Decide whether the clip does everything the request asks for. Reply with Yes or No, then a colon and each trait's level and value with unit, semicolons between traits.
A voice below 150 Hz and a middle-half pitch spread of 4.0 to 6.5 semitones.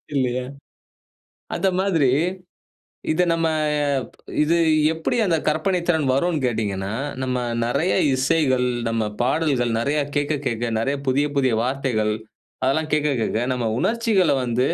Yes: low, 135 Hz; average, 4.7 semitones